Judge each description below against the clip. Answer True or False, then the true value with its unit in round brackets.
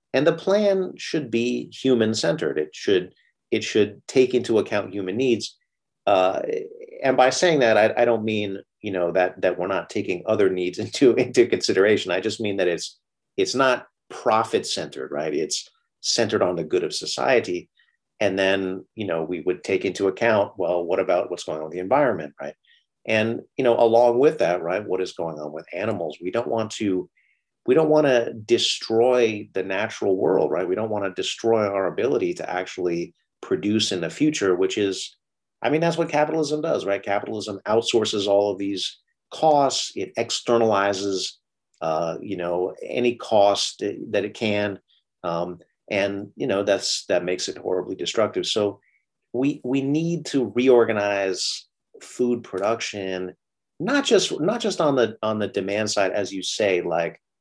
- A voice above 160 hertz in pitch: False (115 Hz)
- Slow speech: False (175 wpm)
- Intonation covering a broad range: True (8.3 semitones)